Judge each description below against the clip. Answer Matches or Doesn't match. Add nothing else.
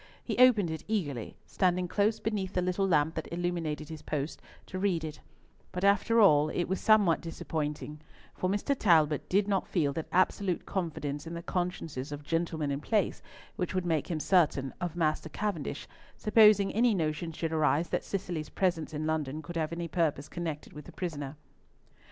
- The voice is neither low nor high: Matches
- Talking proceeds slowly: Doesn't match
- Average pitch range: Matches